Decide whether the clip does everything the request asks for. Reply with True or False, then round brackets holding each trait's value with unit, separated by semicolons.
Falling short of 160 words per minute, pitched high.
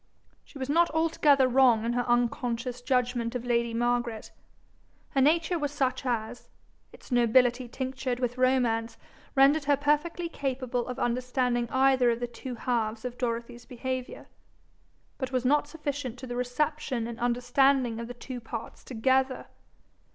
True (150 wpm; 250 Hz)